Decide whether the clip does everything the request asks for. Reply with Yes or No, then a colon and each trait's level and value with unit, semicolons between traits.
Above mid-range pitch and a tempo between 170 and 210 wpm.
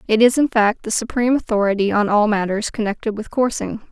Yes: high, 220 Hz; average, 200 wpm